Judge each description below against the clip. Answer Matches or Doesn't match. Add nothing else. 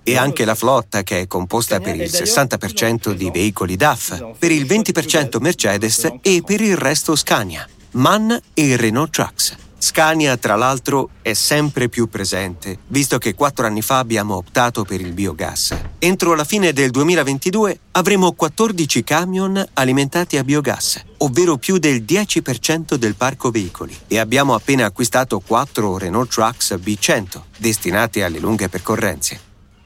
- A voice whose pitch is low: Matches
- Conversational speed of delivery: Matches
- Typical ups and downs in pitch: Doesn't match